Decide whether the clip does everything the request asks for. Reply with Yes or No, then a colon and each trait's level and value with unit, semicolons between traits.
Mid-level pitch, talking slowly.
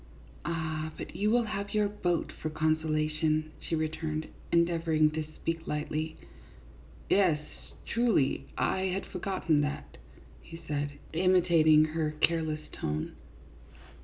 Yes: medium, 160 Hz; slow, 130 wpm